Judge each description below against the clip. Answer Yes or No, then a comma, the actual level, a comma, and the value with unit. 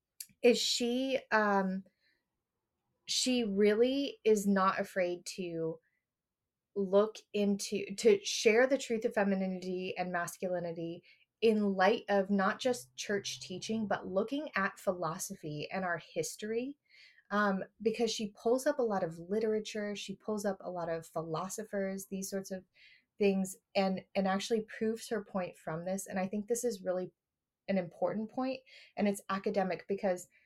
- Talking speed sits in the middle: Yes, average, 145 wpm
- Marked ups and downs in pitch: No, average, 3.1 semitones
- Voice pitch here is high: Yes, high, 200 Hz